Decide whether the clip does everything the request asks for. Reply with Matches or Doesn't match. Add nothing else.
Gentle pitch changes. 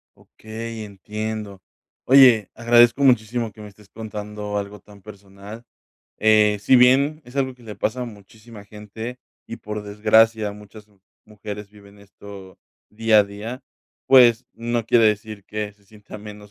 Matches